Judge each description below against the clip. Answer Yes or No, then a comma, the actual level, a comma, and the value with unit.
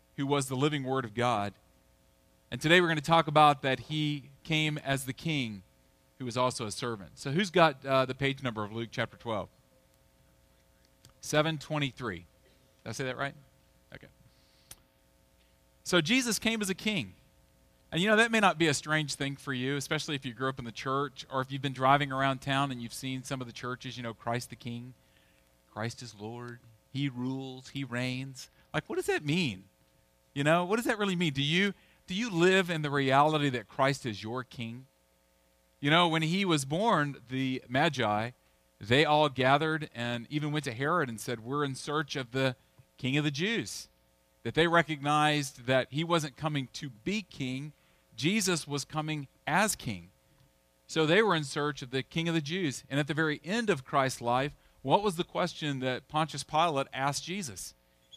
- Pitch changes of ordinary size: Yes, average, 4.5 semitones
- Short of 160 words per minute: No, average, 195 wpm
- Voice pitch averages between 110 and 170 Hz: Yes, low, 135 Hz